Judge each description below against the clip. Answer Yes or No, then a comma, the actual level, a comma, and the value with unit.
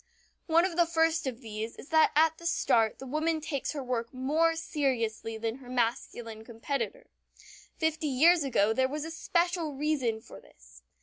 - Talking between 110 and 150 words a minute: No, average, 170 wpm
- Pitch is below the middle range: No, very high, 280 Hz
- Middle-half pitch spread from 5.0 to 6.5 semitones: Yes, wide, 5.5 semitones